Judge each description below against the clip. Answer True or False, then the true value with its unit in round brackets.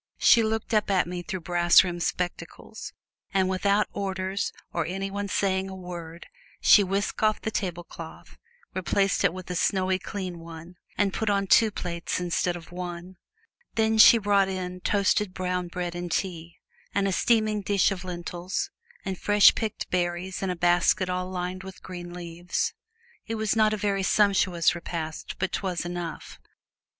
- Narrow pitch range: True (2.2 semitones)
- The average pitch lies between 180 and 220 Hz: True (185 Hz)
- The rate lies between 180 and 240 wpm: False (170 wpm)